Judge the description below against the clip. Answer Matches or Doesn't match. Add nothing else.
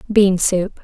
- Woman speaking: Matches